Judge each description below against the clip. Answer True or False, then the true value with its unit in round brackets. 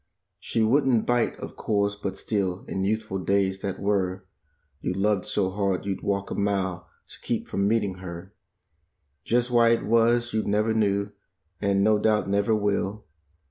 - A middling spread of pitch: False (2.1 semitones)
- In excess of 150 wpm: True (165 wpm)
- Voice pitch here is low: True (100 Hz)